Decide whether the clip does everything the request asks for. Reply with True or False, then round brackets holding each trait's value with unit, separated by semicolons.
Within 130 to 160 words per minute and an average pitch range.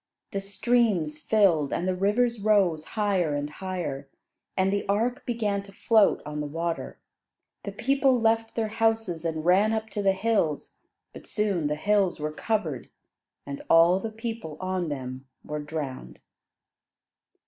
False (150 wpm; 5.8 semitones)